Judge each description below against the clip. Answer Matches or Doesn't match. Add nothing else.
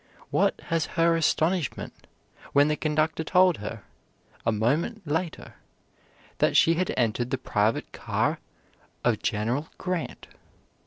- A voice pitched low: Doesn't match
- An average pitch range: Doesn't match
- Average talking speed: Doesn't match